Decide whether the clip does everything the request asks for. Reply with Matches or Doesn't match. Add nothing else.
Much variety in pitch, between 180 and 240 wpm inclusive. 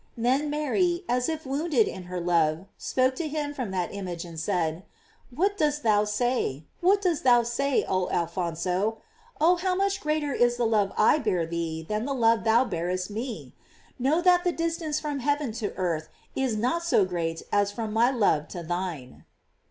Matches